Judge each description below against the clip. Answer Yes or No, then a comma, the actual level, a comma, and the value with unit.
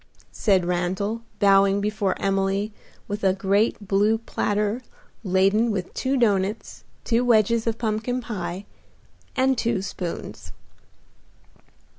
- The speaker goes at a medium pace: No, slow, 110 wpm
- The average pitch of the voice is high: Yes, high, 205 Hz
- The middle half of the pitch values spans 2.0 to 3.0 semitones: Yes, average, 2.7 semitones